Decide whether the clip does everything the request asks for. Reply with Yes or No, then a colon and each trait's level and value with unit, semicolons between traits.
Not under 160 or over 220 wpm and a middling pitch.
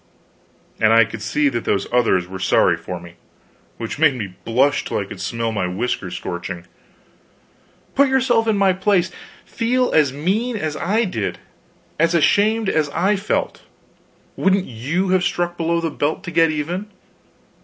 Yes: average, 165 wpm; medium, 160 Hz